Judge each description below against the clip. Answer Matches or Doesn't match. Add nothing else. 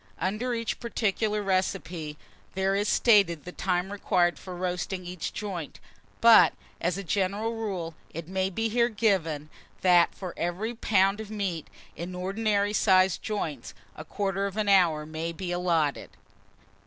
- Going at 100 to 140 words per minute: Doesn't match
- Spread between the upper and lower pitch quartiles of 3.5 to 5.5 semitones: Doesn't match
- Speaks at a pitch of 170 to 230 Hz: Matches